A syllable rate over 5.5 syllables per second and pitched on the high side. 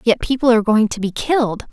Yes: 6.4 syllables/s; high, 230 Hz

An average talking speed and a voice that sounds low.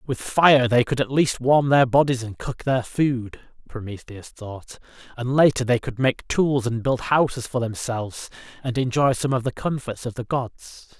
Yes: average, 190 wpm; low, 125 Hz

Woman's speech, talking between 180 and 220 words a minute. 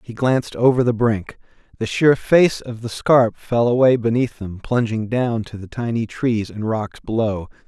No: male; average, 190 wpm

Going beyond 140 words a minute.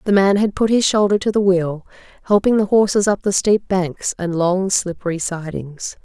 Yes: average, 200 wpm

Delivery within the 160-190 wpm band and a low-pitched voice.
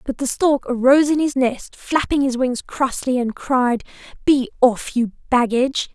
No: average, 170 wpm; very high, 260 Hz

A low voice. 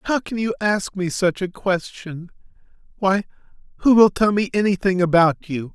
No: high, 190 Hz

